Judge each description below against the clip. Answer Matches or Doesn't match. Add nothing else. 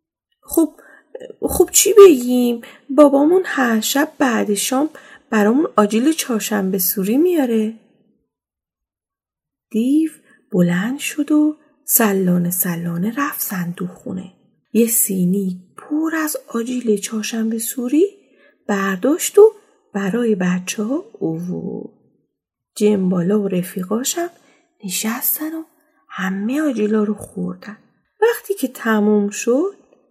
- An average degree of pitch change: Doesn't match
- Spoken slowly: Matches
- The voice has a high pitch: Matches